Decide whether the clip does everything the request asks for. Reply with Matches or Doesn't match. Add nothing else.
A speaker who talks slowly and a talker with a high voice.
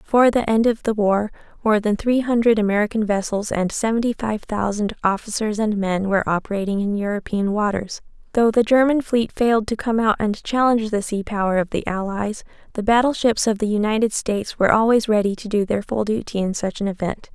Doesn't match